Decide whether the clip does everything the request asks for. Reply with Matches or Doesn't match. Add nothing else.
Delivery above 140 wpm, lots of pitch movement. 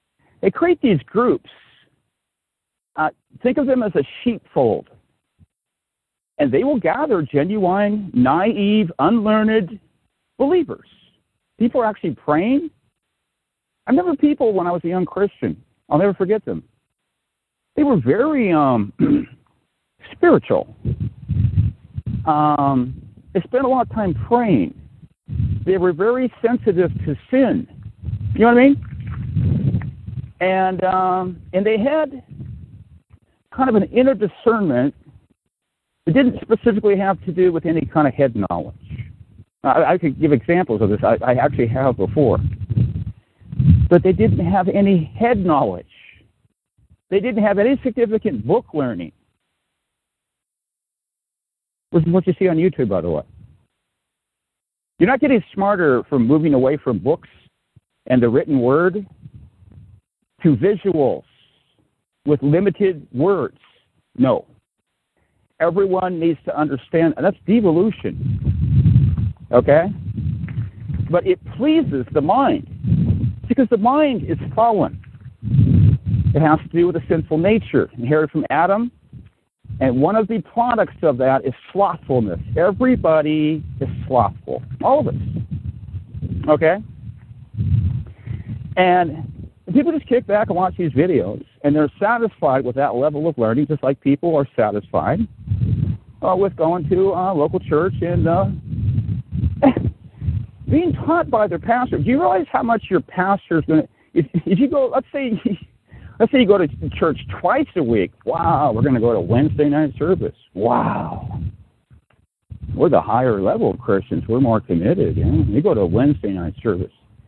Doesn't match